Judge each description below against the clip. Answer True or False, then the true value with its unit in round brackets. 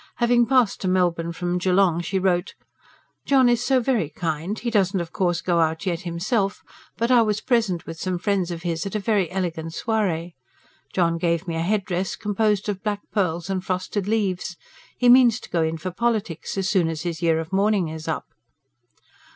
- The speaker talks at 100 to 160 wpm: False (195 wpm)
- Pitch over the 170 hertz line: True (185 Hz)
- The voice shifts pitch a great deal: False (3.8 semitones)